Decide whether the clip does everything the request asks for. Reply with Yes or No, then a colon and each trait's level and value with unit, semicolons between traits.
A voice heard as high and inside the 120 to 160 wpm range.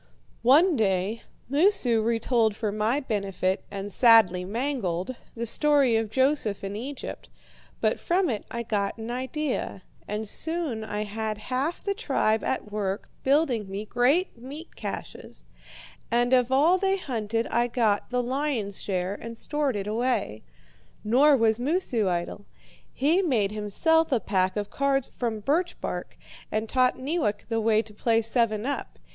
Yes: high, 230 Hz; average, 150 wpm